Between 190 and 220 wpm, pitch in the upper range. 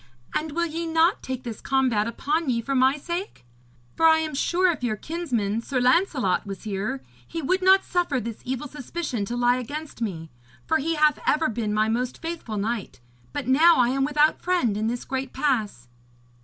Yes: average, 195 wpm; very high, 265 Hz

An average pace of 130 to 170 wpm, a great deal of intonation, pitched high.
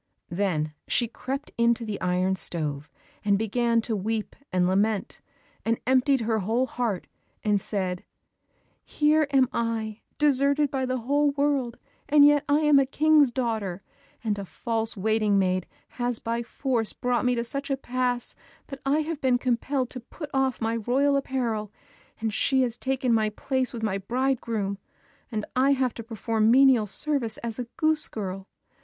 No: average, 165 wpm; average, 3.9 semitones; high, 235 Hz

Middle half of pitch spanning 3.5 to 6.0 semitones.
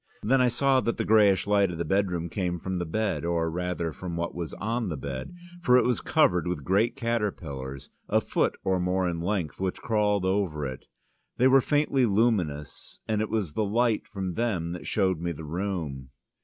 Yes: average, 4.5 semitones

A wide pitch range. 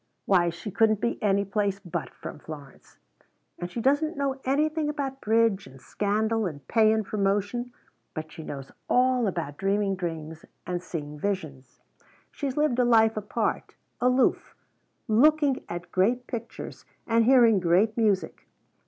Yes: wide, 5.8 semitones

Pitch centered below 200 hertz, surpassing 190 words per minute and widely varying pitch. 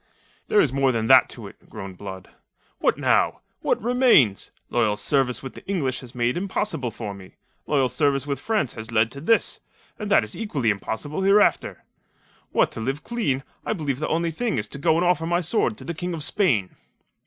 Yes: medium, 140 Hz; average, 200 wpm; wide, 7.3 semitones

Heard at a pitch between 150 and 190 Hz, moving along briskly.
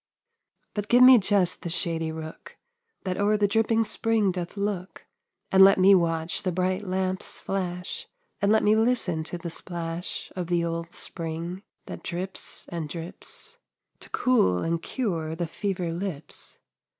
No: medium, 185 Hz; average, 155 wpm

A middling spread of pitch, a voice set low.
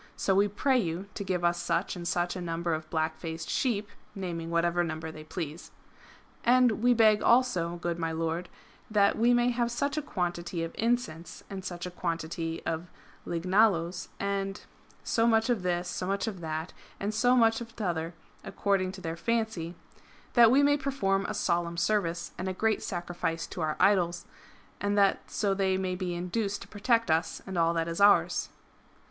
No: average, 4.1 semitones; medium, 185 Hz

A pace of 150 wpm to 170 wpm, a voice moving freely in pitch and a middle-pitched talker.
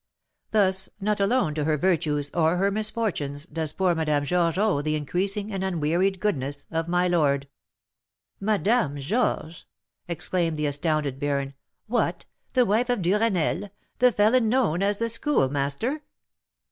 No: average, 140 wpm; wide, 5.7 semitones; medium, 175 Hz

